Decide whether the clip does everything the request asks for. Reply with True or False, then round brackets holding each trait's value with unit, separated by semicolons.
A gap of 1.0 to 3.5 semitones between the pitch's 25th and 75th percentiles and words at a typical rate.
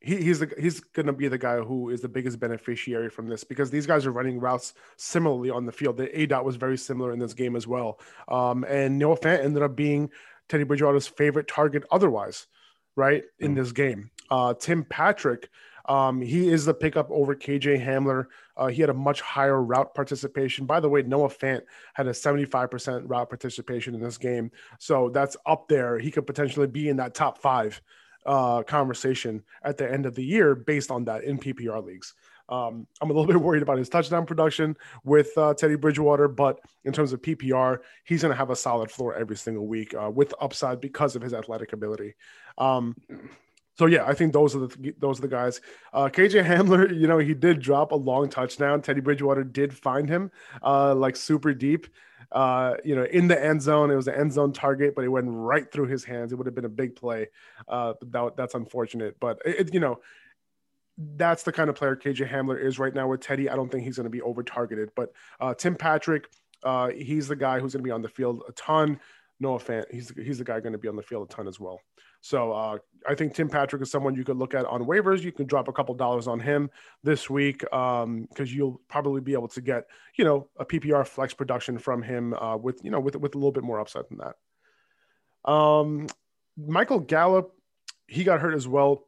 False (2.9 semitones; 225 wpm)